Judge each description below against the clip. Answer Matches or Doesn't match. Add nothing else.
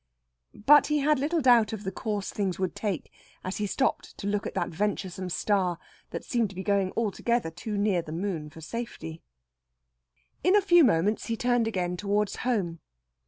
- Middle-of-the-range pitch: Doesn't match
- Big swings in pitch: Doesn't match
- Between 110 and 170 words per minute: Doesn't match